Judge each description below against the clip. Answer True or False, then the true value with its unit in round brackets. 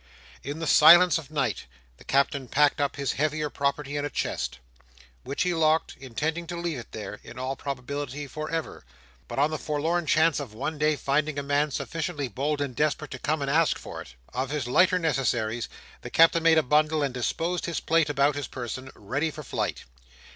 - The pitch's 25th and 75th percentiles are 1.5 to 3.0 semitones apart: True (2.6 semitones)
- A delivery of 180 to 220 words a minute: True (200 wpm)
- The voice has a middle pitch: True (145 Hz)